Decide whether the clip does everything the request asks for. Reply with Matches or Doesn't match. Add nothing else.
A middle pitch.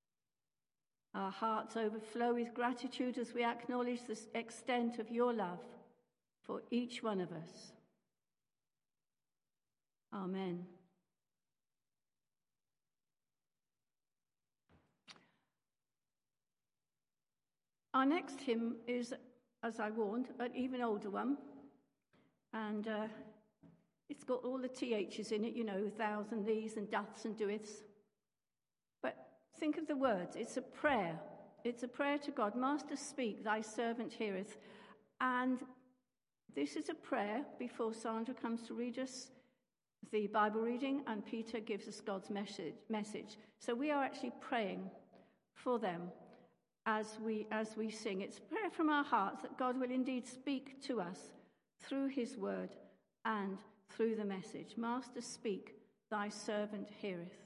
Doesn't match